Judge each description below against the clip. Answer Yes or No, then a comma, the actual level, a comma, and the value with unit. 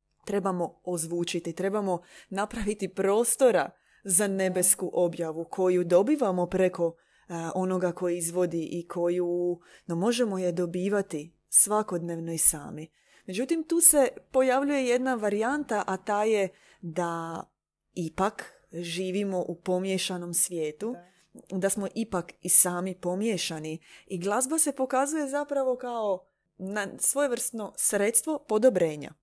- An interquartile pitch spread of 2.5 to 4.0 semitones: No, average, 4.4 semitones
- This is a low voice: No, high, 190 Hz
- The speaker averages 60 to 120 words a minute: Yes, slow, 110 wpm